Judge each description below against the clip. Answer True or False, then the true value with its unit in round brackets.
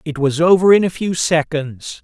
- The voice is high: False (160 Hz)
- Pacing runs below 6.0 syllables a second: True (4.7 syllables/s)